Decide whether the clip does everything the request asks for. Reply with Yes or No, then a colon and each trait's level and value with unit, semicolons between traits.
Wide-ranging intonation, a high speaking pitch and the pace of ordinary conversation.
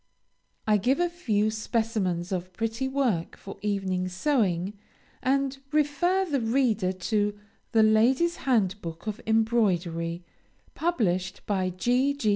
No: wide, 6.0 semitones; high, 215 Hz; slow, 120 wpm